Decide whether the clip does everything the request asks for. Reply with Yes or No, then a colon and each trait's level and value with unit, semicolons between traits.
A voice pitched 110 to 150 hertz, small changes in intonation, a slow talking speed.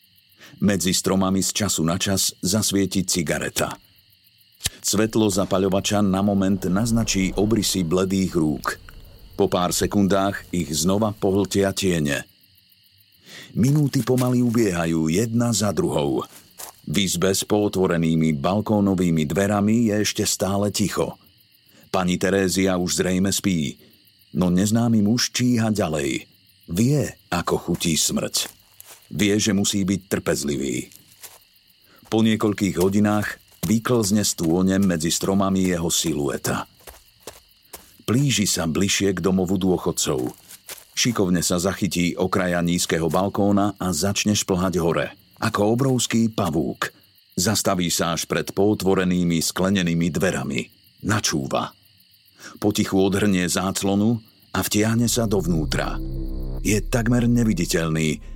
No: low, 100 Hz; narrow, 2.3 semitones; slow, 105 wpm